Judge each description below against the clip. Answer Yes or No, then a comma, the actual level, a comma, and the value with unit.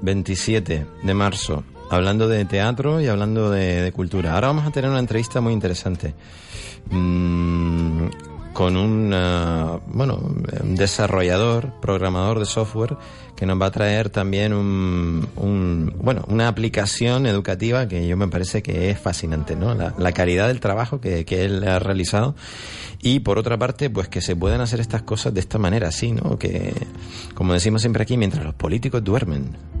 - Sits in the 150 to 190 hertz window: No, low, 100 Hz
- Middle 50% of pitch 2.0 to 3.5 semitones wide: No, average, 3.9 semitones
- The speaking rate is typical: Yes, average, 170 wpm